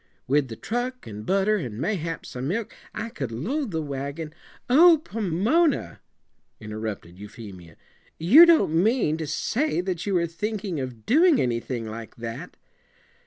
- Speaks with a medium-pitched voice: Yes, medium, 165 Hz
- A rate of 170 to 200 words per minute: No, average, 150 wpm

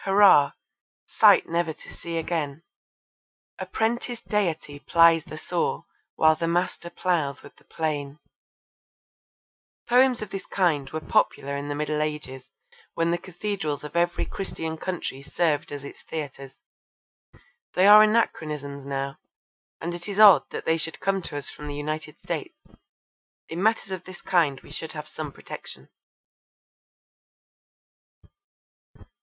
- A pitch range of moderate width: Yes, average, 4.1 semitones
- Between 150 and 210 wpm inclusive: No, average, 140 wpm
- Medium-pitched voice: Yes, medium, 165 Hz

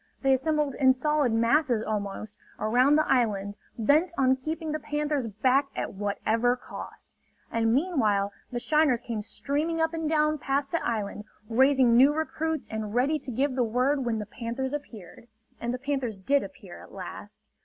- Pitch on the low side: No, very high, 260 Hz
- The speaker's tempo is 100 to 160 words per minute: No, average, 170 wpm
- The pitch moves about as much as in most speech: Yes, average, 4.7 semitones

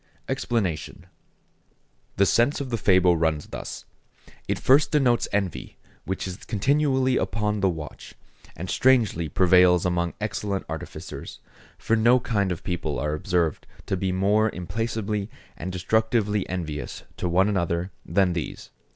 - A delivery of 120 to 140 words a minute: Yes, slow, 135 wpm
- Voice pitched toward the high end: No, very low, 95 Hz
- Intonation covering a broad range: No, average, 4.0 semitones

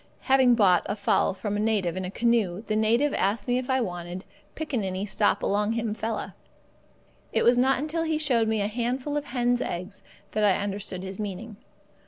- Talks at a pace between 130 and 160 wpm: No, average, 195 wpm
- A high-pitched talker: Yes, high, 220 Hz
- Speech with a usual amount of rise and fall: Yes, average, 3.7 semitones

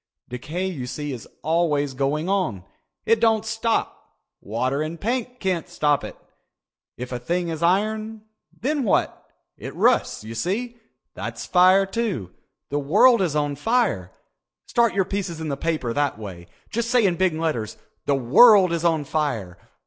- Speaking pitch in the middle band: Yes, medium, 165 Hz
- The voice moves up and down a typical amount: No, wide, 7.2 semitones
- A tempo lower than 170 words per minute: Yes, average, 160 wpm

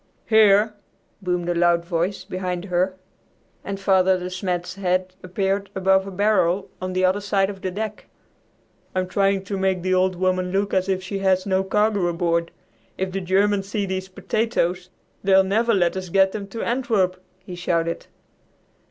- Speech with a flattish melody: Yes, narrow, 1.4 semitones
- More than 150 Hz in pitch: Yes, high, 190 Hz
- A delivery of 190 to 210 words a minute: No, average, 170 wpm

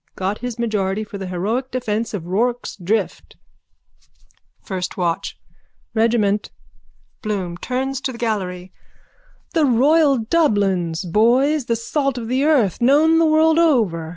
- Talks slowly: Yes, slow, 130 wpm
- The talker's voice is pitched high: Yes, high, 230 Hz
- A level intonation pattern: No, wide, 5.5 semitones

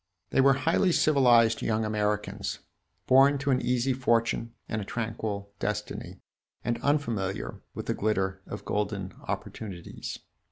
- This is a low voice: Yes, low, 115 Hz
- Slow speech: Yes, slow, 130 wpm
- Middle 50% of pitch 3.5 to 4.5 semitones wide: Yes, average, 4.0 semitones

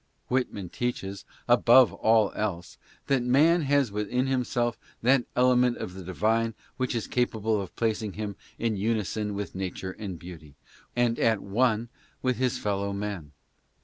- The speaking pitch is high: No, low, 110 Hz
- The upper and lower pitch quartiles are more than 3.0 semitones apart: Yes, average, 3.7 semitones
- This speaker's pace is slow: No, average, 145 wpm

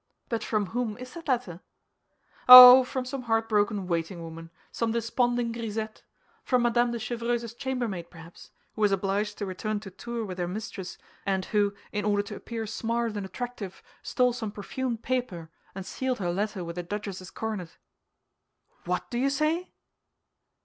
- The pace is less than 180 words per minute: Yes, average, 165 wpm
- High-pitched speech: Yes, high, 220 Hz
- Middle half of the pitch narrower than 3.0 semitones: No, average, 3.8 semitones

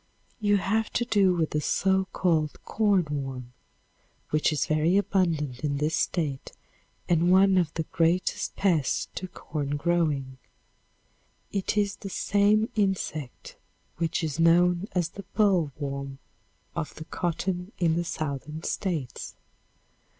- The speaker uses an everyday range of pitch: Yes, average, 4.0 semitones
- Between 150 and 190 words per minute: No, slow, 135 wpm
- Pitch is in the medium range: Yes, medium, 170 Hz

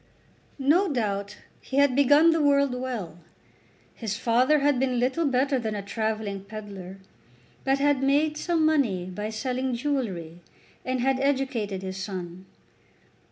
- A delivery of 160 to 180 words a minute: No, average, 140 wpm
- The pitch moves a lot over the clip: Yes, wide, 5.7 semitones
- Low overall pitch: No, very high, 250 Hz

